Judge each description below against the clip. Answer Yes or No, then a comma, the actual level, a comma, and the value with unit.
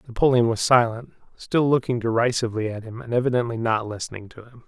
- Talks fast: No, average, 180 wpm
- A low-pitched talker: Yes, low, 115 Hz